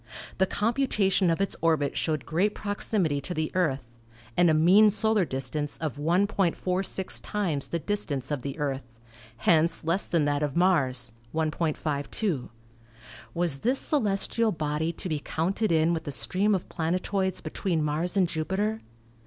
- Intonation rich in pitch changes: No, average, 4.5 semitones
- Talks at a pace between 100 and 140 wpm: No, average, 155 wpm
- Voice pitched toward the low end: No, medium, 170 Hz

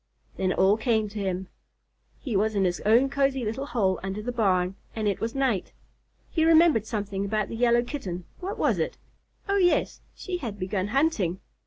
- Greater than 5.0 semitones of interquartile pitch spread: Yes, wide, 5.4 semitones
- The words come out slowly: No, average, 190 wpm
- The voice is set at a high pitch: Yes, high, 220 Hz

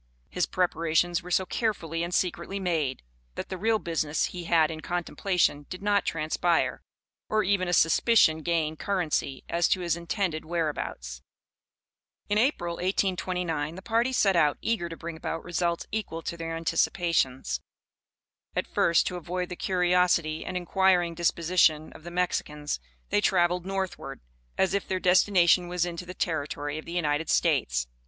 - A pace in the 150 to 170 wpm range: Yes, average, 155 wpm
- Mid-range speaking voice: Yes, medium, 175 Hz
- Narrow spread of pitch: Yes, narrow, 2.3 semitones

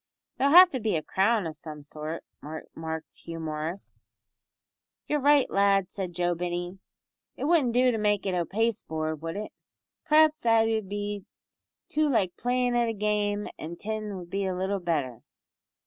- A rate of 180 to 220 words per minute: No, average, 165 wpm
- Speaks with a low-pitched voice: No, high, 200 Hz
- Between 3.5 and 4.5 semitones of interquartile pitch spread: No, average, 5.2 semitones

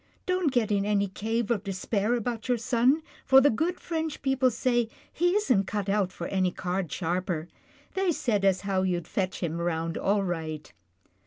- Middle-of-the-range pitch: No, high, 205 Hz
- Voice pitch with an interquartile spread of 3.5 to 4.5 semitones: No, average, 5.3 semitones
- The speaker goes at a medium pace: Yes, average, 180 wpm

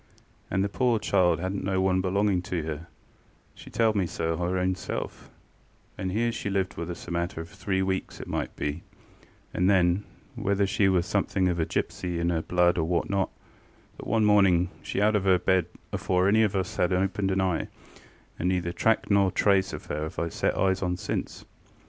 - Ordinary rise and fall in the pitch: No, narrow, 2.1 semitones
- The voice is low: Yes, very low, 95 Hz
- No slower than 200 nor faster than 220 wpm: Yes, fast, 205 wpm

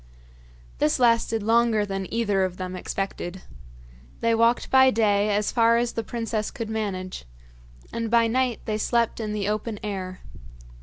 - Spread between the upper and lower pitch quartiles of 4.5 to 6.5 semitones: No, narrow, 2.5 semitones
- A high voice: Yes, high, 220 Hz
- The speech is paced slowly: No, average, 155 wpm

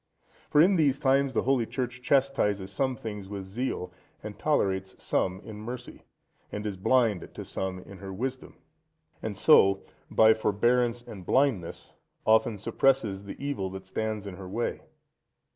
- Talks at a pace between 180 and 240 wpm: No, average, 155 wpm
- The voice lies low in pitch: Yes, low, 110 Hz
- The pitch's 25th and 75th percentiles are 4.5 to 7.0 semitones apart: Yes, average, 4.9 semitones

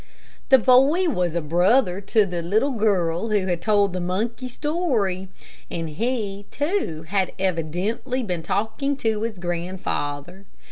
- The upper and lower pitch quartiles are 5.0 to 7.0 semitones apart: Yes, average, 5.3 semitones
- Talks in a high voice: Yes, high, 200 Hz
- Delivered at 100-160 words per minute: Yes, average, 140 wpm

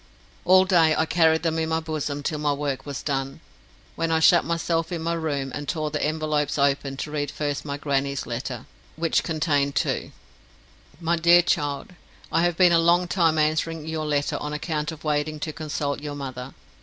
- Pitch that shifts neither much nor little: No, narrow, 2.3 semitones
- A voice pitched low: No, medium, 155 Hz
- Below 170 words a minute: No, average, 195 wpm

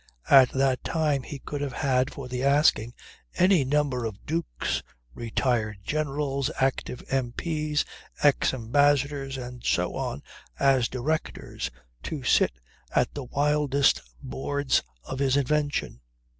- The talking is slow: Yes, slow, 125 wpm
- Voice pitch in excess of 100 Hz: Yes, low, 135 Hz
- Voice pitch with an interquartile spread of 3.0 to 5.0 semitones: No, narrow, 2.4 semitones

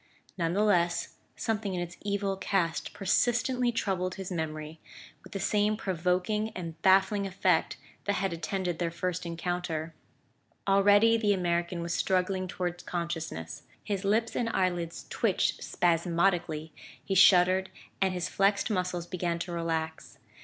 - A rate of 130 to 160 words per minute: Yes, average, 140 wpm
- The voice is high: No, medium, 180 Hz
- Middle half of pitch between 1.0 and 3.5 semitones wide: Yes, narrow, 2.6 semitones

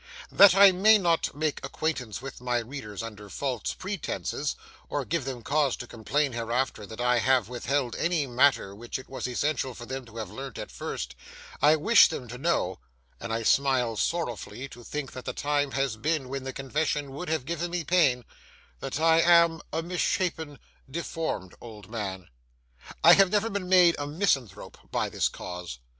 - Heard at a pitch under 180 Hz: Yes, low, 135 Hz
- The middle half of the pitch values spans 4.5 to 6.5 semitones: Yes, wide, 5.4 semitones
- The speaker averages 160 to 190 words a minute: Yes, average, 175 wpm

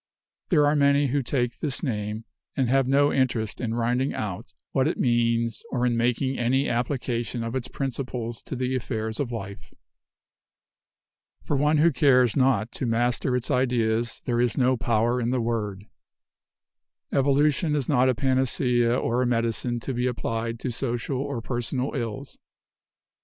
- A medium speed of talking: Yes, average, 160 wpm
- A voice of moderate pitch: No, low, 125 Hz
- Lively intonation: No, narrow, 2.4 semitones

